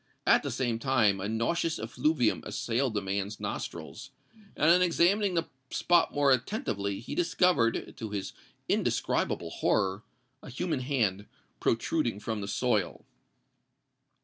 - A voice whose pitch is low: Yes, low, 120 Hz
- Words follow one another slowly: Yes, slow, 120 wpm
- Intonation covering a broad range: Yes, wide, 7.0 semitones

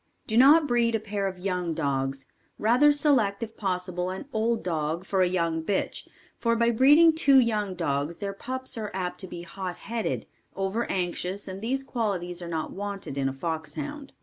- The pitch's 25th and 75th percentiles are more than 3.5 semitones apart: Yes, average, 4.9 semitones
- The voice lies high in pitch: Yes, high, 195 Hz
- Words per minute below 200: Yes, average, 185 wpm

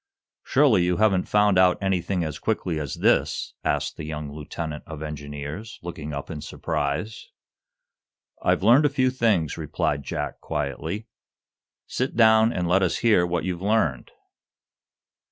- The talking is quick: No, average, 145 wpm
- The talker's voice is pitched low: Yes, very low, 90 Hz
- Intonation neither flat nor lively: No, wide, 6.1 semitones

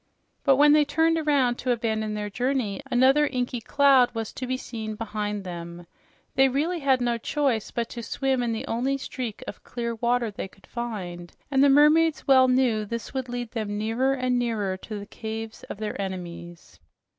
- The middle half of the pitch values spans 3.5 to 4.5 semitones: Yes, average, 3.8 semitones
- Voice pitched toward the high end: Yes, high, 240 Hz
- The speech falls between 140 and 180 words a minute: No, average, 190 wpm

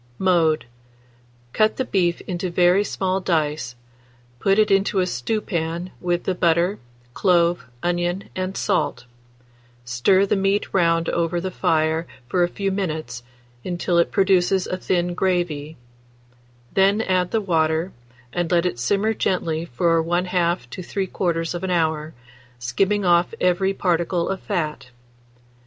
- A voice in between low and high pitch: Yes, medium, 175 Hz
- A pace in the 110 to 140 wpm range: Yes, slow, 135 wpm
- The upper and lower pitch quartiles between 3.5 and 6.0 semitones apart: No, narrow, 2.4 semitones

